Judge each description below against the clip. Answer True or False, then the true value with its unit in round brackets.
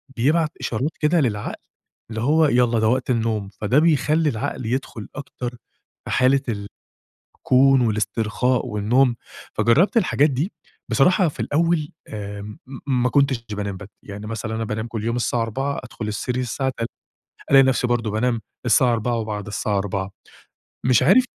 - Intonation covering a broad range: False (4.0 semitones)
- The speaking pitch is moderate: False (120 Hz)